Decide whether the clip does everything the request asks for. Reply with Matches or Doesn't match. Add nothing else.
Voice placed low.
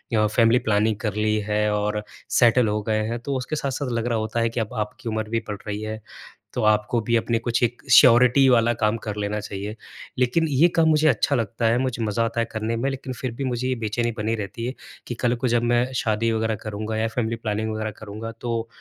Matches